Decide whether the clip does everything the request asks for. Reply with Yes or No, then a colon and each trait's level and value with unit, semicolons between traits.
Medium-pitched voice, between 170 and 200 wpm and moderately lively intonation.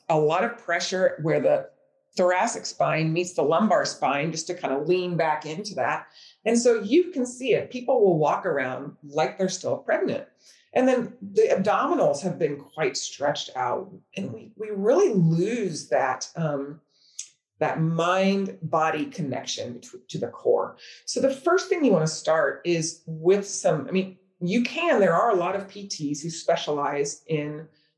No: medium, 180 Hz; average, 175 wpm; wide, 6.0 semitones